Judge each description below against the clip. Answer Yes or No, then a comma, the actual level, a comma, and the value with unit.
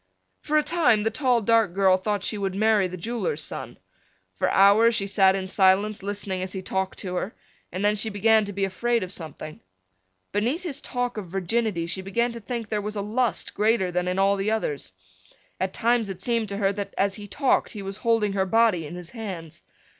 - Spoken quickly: Yes, fast, 215 wpm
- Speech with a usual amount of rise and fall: Yes, average, 3.0 semitones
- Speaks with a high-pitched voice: Yes, high, 205 Hz